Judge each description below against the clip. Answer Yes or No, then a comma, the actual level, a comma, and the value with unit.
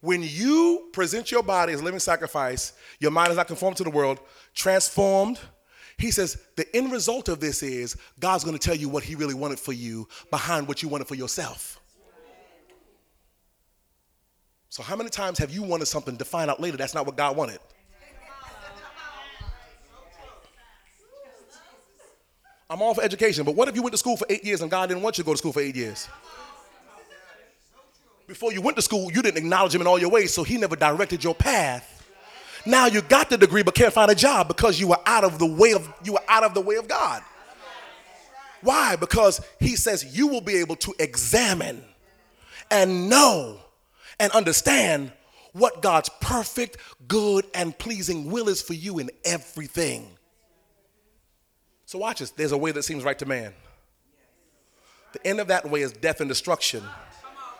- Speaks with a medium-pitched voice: Yes, medium, 180 Hz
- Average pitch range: No, wide, 6.3 semitones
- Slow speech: No, average, 175 wpm